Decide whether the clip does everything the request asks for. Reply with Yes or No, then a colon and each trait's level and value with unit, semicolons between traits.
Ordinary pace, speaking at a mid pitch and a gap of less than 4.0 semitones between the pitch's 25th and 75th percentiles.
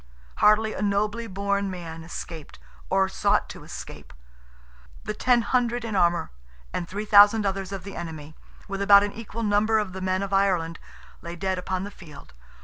No: average, 175 wpm; high, 195 Hz; narrow, 2.4 semitones